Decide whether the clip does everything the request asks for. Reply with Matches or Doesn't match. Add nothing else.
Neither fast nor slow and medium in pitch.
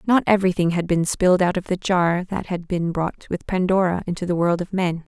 Doesn't match